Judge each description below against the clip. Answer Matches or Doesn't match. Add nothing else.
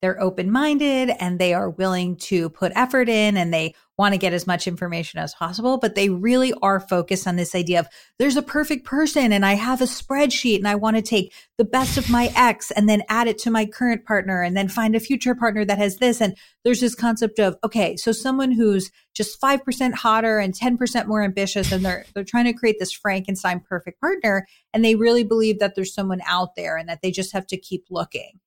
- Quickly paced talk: Matches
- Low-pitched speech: Doesn't match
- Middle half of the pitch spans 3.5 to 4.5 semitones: Matches